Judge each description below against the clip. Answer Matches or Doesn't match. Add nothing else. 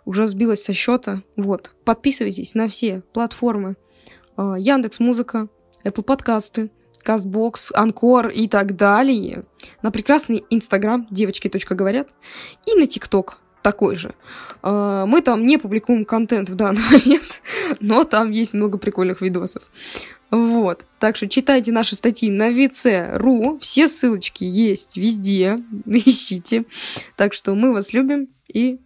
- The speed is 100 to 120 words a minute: Doesn't match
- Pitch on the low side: Doesn't match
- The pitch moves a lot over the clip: Doesn't match